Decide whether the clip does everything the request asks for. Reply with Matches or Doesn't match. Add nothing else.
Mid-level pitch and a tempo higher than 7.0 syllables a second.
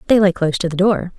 Matches